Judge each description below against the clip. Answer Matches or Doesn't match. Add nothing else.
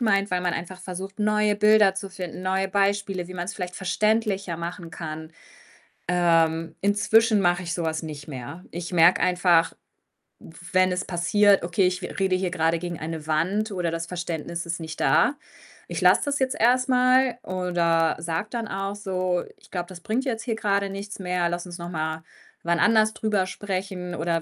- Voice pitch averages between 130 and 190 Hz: Matches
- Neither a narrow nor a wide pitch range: Matches